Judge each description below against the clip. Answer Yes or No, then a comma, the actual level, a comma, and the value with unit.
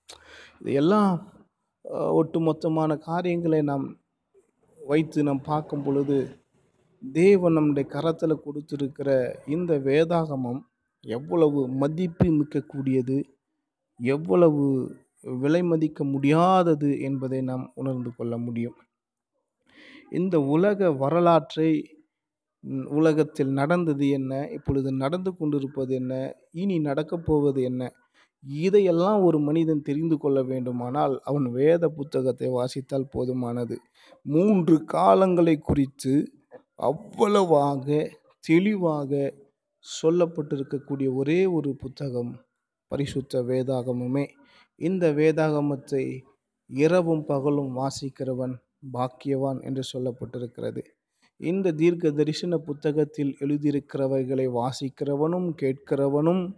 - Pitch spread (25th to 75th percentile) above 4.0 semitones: No, average, 3.4 semitones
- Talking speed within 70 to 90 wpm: Yes, average, 80 wpm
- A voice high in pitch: No, medium, 145 Hz